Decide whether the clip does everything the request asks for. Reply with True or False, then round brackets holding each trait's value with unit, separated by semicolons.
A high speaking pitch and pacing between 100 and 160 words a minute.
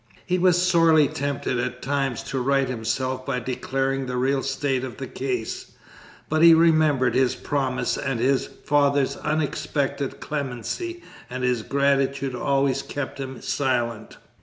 False (135 Hz; 140 wpm)